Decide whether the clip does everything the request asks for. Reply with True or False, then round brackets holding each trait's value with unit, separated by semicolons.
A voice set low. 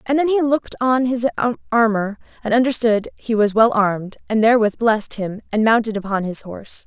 False (225 Hz)